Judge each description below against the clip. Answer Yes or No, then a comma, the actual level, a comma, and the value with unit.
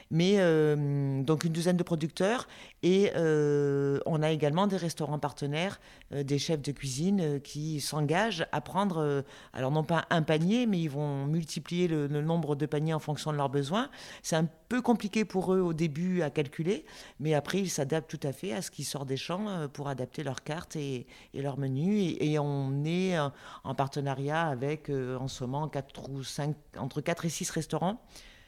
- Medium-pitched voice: Yes, medium, 155 Hz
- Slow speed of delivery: No, average, 200 wpm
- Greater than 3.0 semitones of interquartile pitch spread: Yes, average, 3.4 semitones